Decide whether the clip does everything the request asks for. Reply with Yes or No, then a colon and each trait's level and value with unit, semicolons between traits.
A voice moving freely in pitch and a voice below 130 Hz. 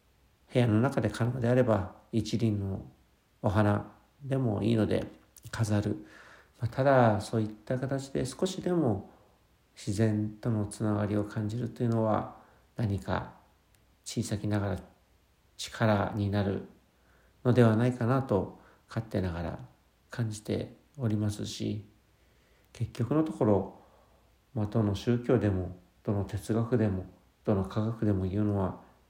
No: average, 2.7 semitones; low, 105 Hz